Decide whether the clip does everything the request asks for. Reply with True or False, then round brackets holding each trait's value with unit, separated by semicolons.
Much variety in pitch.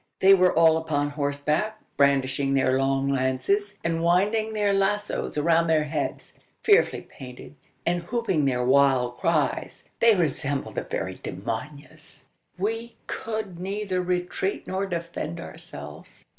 True (5.8 semitones)